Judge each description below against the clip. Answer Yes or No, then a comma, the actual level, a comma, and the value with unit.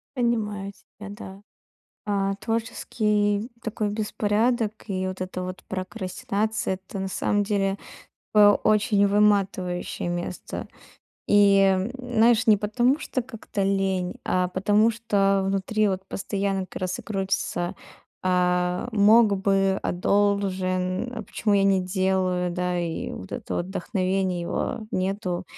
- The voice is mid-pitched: No, high, 195 Hz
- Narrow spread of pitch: Yes, narrow, 2.1 semitones